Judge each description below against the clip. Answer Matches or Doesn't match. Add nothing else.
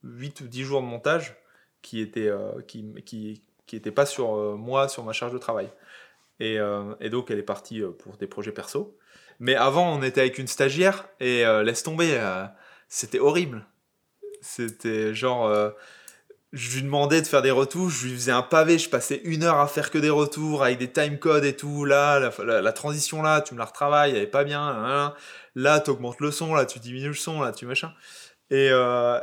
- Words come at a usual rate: Doesn't match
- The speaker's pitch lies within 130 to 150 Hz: Matches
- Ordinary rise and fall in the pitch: Matches